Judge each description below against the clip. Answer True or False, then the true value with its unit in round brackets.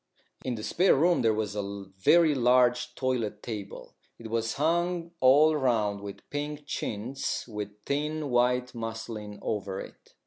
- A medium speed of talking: True (145 wpm)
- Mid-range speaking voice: False (120 Hz)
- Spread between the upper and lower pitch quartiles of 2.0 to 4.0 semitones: False (5.4 semitones)